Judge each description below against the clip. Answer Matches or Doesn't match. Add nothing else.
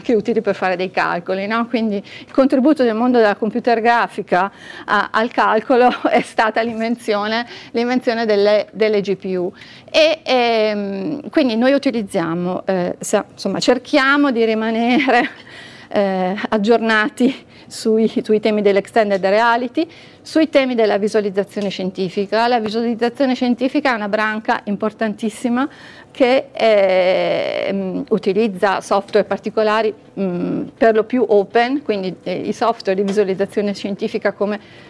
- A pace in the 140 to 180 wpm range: Doesn't match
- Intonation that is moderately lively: Matches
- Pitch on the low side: Doesn't match